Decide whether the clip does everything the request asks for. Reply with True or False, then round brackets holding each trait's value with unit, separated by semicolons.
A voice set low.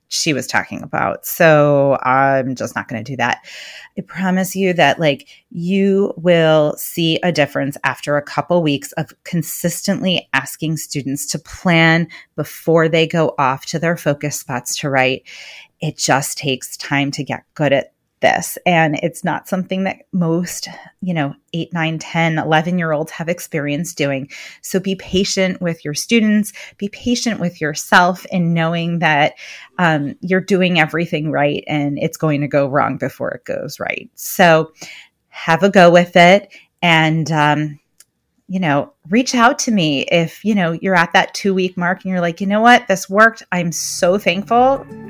False (165 Hz)